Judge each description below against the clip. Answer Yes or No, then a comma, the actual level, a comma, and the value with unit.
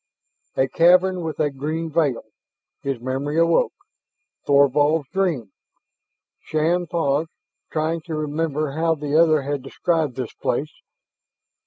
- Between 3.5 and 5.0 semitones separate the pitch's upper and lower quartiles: No, average, 2.8 semitones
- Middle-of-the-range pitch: Yes, medium, 155 Hz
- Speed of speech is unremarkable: No, slow, 120 wpm